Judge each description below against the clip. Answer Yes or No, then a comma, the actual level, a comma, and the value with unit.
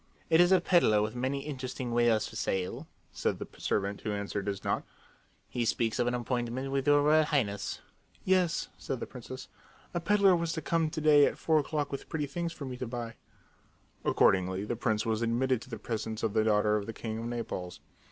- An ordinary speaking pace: No, fast, 210 wpm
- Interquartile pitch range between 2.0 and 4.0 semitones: No, average, 5.2 semitones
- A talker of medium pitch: No, low, 120 Hz